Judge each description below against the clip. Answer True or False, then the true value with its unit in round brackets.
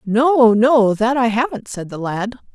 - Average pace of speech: True (190 wpm)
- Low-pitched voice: False (230 Hz)